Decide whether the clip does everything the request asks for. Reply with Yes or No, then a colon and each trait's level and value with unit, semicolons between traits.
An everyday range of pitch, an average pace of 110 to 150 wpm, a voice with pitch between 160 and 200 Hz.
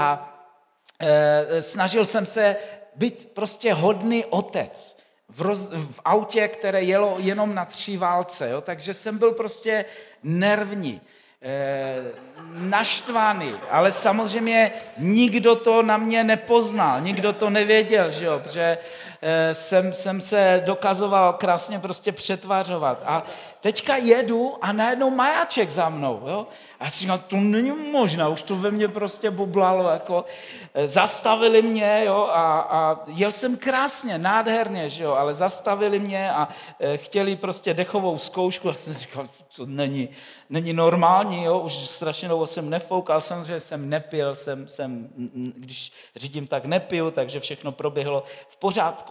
Yes: average, 5.0 semitones; average, 145 wpm; medium, 185 Hz